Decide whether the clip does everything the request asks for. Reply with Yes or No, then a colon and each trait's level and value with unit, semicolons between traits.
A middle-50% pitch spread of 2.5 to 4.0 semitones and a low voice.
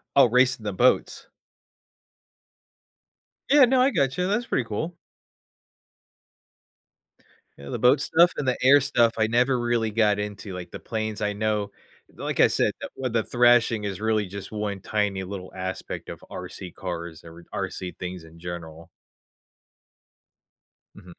No: average, 5.0 semitones; low, 110 Hz